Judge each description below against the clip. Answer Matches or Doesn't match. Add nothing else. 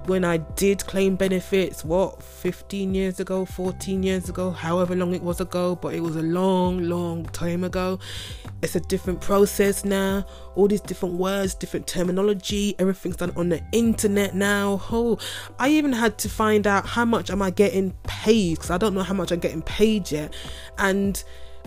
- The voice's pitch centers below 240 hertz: Matches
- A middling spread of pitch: Doesn't match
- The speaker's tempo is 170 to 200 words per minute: Matches